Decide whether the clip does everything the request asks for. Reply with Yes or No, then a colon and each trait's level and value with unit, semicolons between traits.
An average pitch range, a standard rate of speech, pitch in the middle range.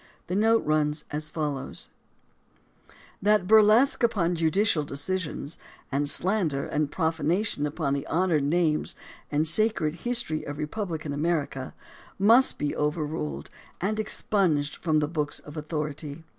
No: average, 4.3 semitones; slow, 130 wpm; medium, 155 Hz